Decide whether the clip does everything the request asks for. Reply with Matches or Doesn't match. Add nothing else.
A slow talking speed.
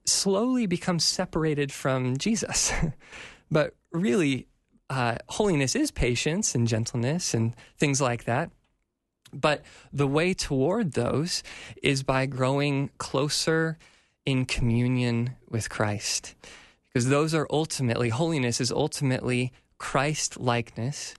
Matches